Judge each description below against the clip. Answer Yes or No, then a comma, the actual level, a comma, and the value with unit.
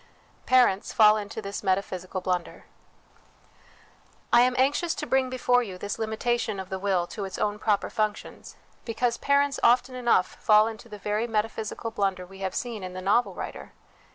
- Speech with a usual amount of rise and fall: Yes, average, 3.8 semitones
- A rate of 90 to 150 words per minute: No, average, 170 wpm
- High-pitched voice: Yes, high, 215 Hz